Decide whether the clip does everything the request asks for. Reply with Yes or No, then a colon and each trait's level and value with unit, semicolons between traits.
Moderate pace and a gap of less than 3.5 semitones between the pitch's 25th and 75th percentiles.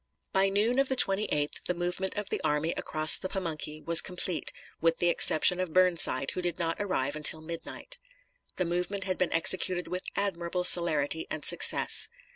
Yes: average, 175 wpm; average, 2.8 semitones